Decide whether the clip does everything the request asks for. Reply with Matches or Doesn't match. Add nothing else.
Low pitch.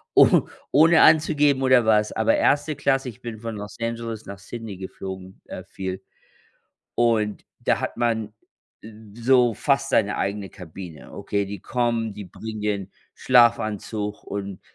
Matches